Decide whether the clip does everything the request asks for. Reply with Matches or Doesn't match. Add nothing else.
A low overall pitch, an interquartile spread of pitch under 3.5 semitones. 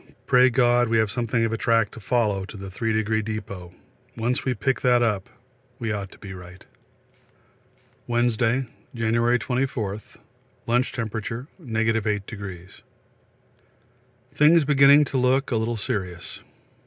Matches